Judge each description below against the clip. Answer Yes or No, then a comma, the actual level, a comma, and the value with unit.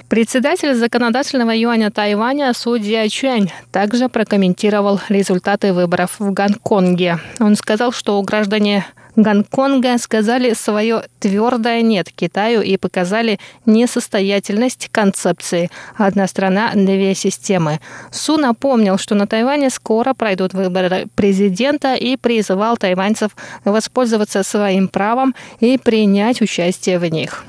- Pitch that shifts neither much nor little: Yes, average, 3.4 semitones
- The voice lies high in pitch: Yes, high, 215 Hz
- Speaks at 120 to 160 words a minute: No, slow, 110 wpm